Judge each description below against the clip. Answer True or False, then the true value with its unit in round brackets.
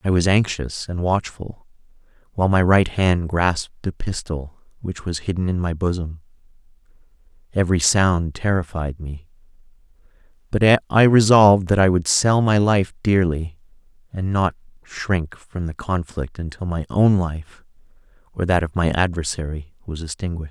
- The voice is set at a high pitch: False (90 Hz)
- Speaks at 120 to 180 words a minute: True (145 wpm)